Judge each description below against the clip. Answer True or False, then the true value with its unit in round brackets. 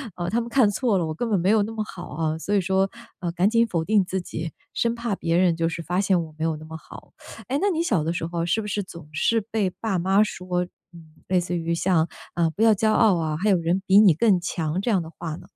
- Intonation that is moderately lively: True (4.0 semitones)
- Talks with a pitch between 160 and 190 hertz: True (185 Hz)